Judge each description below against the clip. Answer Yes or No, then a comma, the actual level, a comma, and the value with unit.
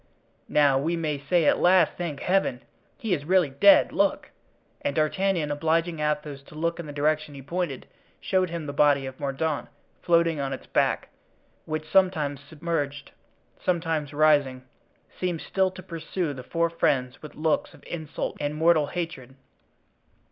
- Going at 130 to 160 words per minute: Yes, average, 155 wpm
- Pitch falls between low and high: Yes, medium, 155 Hz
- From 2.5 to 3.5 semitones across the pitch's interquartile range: Yes, average, 3.0 semitones